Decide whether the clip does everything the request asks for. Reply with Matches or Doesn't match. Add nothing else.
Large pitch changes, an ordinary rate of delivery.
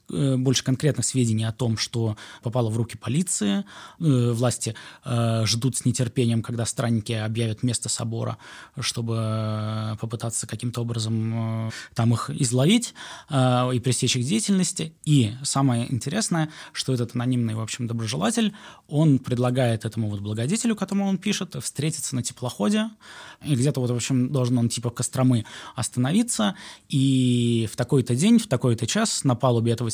Doesn't match